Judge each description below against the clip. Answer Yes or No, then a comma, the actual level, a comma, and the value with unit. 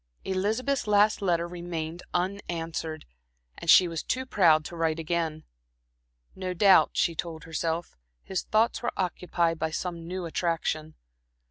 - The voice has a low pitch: No, medium, 170 Hz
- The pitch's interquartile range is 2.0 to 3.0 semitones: Yes, narrow, 2.5 semitones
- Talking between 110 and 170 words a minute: Yes, slow, 135 wpm